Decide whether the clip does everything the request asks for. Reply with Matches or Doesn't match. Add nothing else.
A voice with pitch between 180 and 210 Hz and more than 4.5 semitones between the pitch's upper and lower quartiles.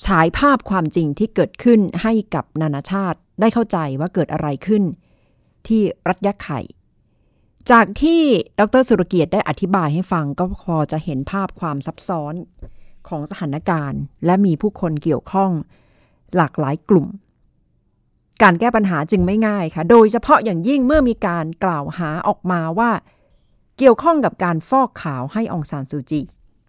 Matches